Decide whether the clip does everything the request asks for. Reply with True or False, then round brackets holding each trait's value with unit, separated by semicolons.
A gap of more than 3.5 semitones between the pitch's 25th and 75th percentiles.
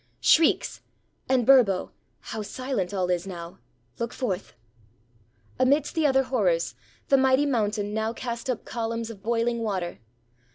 True (4.6 semitones)